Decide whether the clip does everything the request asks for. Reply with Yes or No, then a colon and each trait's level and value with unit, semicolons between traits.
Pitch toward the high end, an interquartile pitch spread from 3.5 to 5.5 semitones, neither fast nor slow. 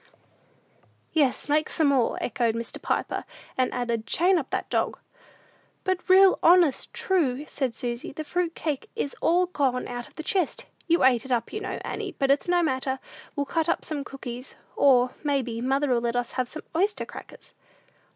Yes: very high, 275 Hz; average, 5.1 semitones; average, 180 wpm